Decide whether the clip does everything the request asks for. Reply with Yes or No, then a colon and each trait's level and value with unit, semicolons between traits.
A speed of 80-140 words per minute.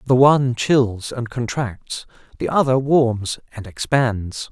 Yes: slow, 135 wpm